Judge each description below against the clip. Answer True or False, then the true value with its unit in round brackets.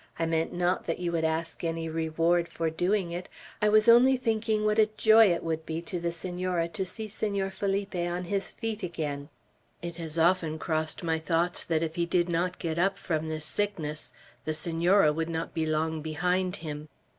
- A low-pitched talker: False (170 Hz)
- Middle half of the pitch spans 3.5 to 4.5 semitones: False (3.0 semitones)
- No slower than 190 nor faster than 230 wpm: True (195 wpm)